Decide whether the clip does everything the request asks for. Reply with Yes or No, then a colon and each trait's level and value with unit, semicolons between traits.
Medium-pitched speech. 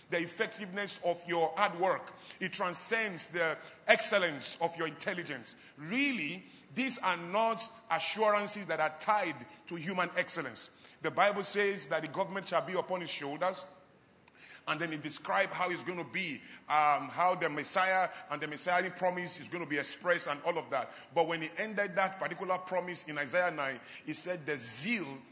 Yes: medium, 180 Hz